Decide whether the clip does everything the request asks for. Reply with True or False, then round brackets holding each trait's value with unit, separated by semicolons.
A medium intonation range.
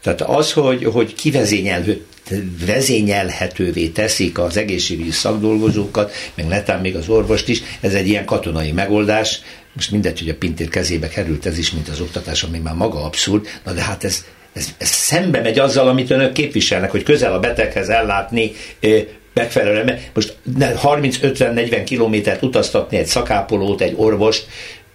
True (4.0 semitones)